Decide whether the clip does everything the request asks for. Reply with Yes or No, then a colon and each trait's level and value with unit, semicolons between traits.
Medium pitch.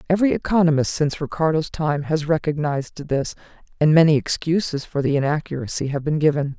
Yes: medium, 150 Hz